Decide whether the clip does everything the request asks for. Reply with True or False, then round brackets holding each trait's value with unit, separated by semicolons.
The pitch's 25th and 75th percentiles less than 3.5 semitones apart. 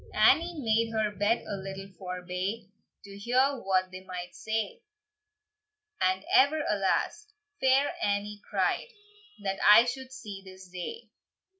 False (4.9 semitones)